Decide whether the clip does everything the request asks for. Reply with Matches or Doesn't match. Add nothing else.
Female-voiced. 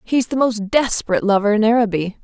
Matches